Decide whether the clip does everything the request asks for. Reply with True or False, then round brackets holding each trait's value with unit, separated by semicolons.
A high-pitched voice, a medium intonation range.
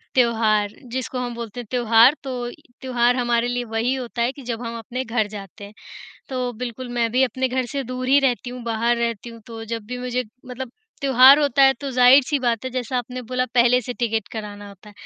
False (245 Hz; 1.7 semitones)